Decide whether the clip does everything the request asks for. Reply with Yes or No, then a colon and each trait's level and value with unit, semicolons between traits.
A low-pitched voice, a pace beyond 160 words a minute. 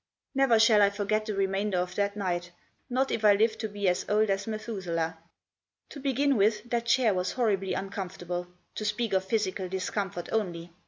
No: high, 205 Hz; average, 180 wpm